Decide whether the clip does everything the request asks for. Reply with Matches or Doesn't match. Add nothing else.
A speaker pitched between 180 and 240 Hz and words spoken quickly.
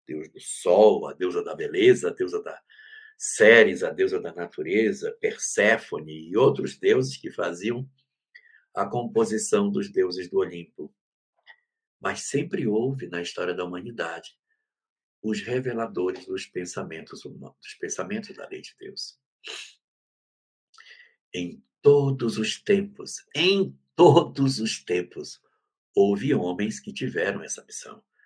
Doesn't match